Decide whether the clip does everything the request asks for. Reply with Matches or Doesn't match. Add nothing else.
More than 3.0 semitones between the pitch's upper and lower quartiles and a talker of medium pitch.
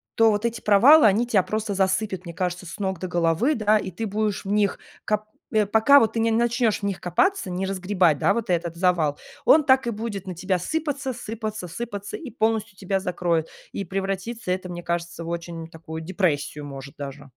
Doesn't match